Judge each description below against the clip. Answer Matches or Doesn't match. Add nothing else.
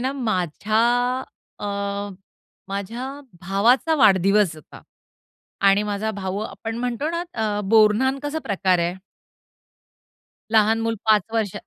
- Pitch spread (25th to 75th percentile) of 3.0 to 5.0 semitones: Matches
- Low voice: Doesn't match